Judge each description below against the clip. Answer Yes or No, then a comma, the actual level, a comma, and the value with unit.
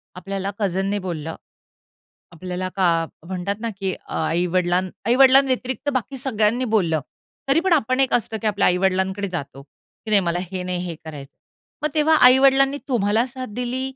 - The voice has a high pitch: Yes, high, 200 Hz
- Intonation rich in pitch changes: Yes, wide, 6.1 semitones